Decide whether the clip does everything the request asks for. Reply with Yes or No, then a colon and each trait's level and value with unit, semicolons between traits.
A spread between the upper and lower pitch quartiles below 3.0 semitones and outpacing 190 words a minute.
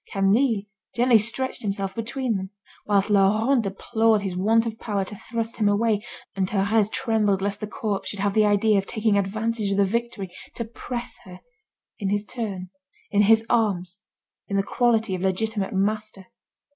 No: narrow, 2.4 semitones; average, 170 wpm